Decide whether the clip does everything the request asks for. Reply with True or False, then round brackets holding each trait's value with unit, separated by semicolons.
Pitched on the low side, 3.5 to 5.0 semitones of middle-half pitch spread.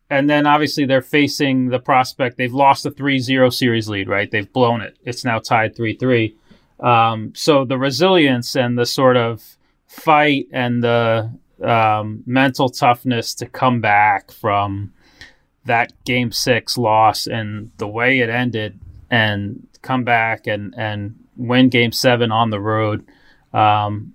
False (120 Hz; 3.1 semitones)